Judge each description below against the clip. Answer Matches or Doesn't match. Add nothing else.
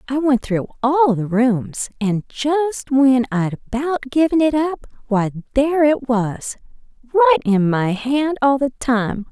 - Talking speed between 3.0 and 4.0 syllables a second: Matches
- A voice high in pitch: Matches